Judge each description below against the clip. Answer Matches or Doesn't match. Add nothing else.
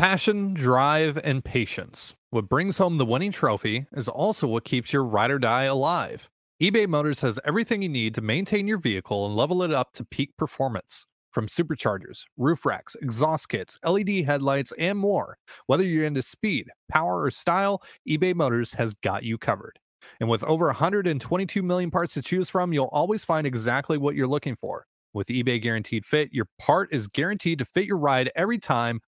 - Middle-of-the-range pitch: Matches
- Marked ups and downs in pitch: Matches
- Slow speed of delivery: Doesn't match